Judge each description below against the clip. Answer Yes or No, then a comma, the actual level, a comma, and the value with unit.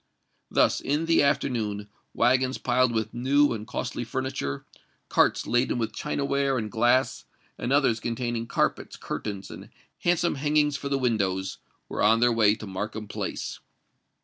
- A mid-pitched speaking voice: No, low, 120 Hz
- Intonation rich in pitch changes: No, average, 3.9 semitones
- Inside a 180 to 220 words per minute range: No, average, 150 wpm